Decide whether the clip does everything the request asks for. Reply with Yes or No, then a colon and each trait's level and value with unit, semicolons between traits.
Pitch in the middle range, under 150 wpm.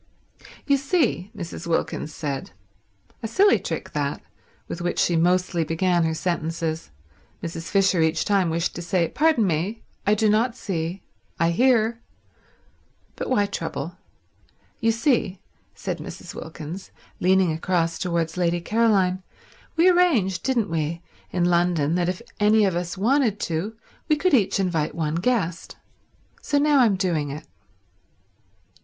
Yes: medium, 180 Hz; slow, 135 wpm